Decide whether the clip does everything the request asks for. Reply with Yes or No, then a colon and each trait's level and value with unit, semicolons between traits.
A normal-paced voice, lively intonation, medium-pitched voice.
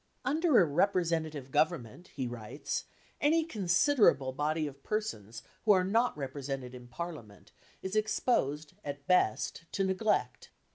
No: slow, 130 wpm; wide, 7.1 semitones; medium, 155 Hz